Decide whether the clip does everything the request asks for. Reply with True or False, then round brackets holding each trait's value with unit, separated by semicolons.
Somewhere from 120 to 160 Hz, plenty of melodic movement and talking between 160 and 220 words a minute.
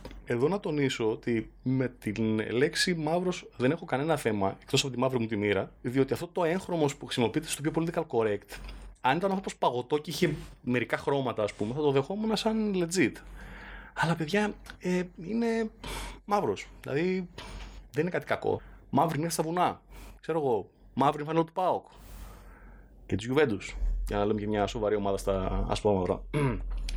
True (135 Hz; 8.2 semitones; 170 wpm)